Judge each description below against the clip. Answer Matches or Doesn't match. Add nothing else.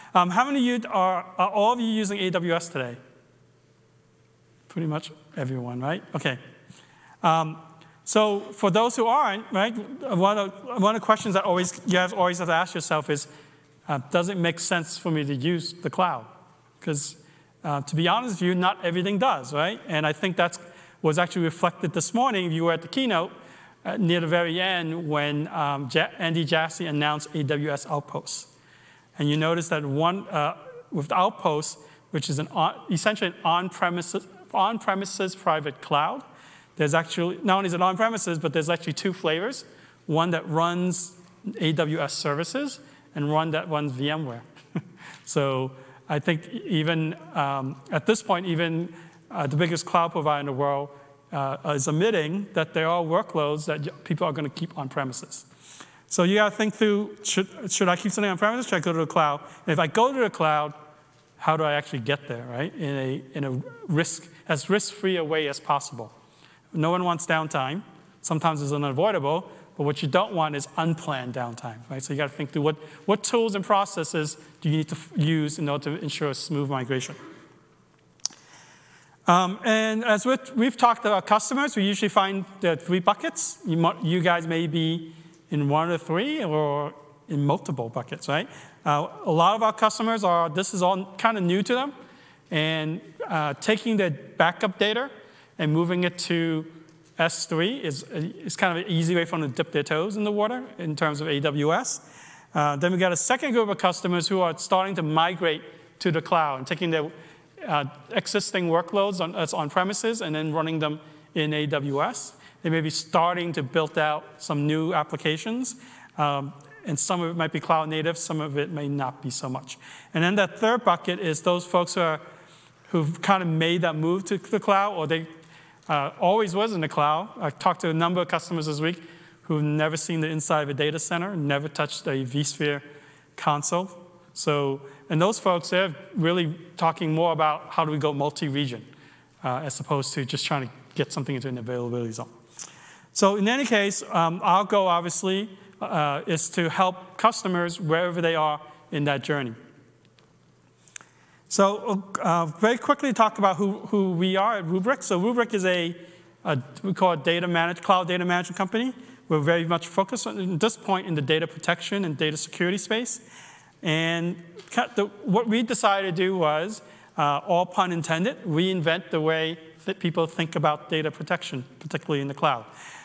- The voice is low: Doesn't match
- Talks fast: Doesn't match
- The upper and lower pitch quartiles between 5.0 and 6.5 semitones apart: Doesn't match